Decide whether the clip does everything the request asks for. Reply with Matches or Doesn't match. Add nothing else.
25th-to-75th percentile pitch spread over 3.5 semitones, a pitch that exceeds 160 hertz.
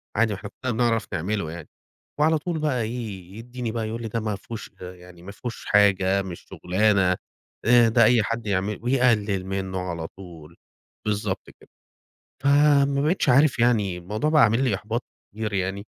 Doesn't match